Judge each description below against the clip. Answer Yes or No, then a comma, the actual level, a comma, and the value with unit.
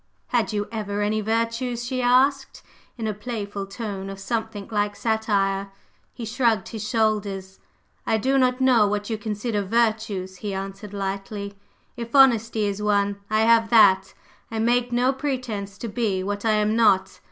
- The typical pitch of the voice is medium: No, high, 215 Hz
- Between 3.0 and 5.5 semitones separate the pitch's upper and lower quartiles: No, narrow, 2.6 semitones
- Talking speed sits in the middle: Yes, average, 165 wpm